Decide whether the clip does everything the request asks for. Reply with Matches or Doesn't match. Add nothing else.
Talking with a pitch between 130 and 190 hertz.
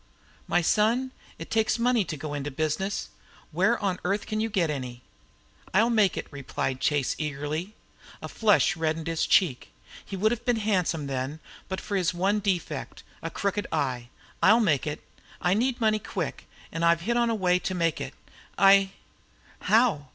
Matches